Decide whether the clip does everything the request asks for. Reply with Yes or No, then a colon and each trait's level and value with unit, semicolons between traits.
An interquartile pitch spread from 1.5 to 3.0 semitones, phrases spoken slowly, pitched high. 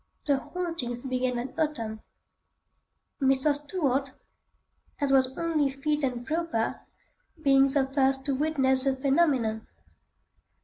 Yes: narrow, 2.4 semitones; slow, 115 wpm; very high, 270 Hz